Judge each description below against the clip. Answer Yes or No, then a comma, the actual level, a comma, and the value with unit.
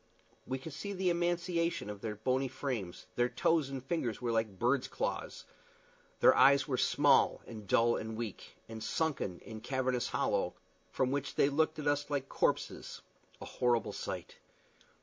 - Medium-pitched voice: No, low, 130 Hz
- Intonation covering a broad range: No, average, 4.3 semitones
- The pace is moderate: Yes, average, 165 wpm